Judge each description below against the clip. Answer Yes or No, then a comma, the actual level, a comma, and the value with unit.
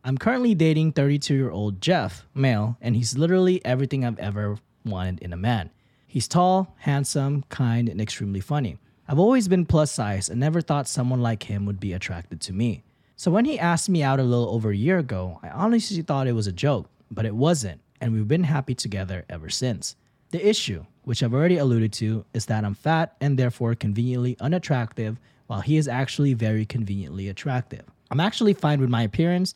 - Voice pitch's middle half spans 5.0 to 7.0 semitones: Yes, wide, 5.5 semitones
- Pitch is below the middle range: Yes, low, 125 Hz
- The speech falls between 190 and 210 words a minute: Yes, average, 200 wpm